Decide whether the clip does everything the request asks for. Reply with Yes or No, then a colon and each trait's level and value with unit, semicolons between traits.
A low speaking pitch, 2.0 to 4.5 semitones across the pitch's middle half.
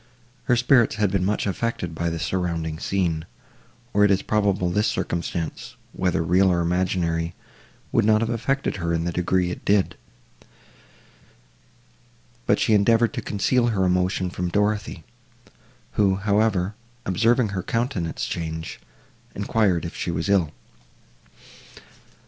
Yes: very low, 95 Hz; average, 3.5 semitones